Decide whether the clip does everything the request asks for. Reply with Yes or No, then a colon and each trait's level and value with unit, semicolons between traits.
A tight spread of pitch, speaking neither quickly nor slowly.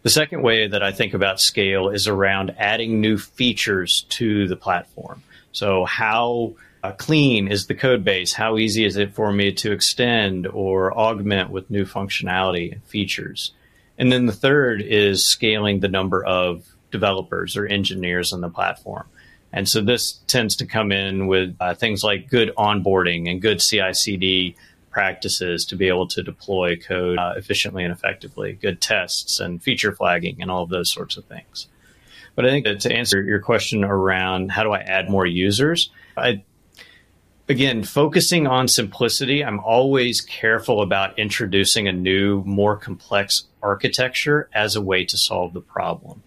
No: average, 3.1 semitones; average, 170 wpm